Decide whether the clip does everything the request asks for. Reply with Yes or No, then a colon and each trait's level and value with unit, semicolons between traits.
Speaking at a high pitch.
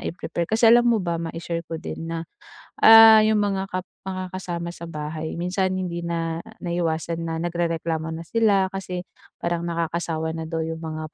No: medium, 170 Hz